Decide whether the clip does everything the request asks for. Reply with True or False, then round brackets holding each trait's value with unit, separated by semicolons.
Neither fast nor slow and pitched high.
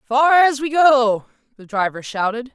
True (165 wpm; 250 Hz)